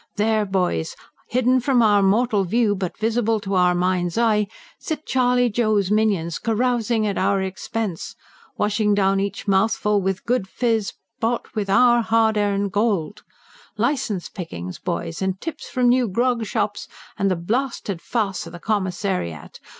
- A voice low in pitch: No, high, 210 Hz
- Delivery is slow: No, average, 150 wpm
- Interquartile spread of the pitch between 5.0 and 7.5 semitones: No, average, 3.4 semitones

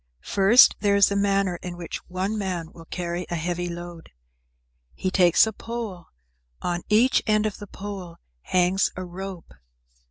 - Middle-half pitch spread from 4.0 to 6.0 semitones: No, narrow, 2.5 semitones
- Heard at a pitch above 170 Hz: Yes, medium, 185 Hz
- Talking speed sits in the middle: Yes, average, 160 wpm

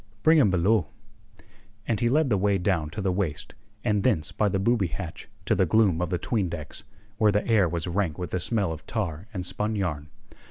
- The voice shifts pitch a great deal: No, average, 3.9 semitones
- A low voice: Yes, very low, 95 Hz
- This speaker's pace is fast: Yes, fast, 215 wpm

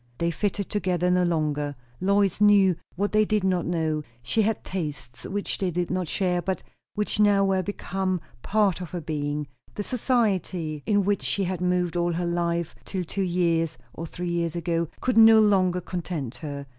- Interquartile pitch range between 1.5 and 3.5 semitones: Yes, average, 2.9 semitones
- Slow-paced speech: No, average, 180 wpm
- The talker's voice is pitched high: No, medium, 180 Hz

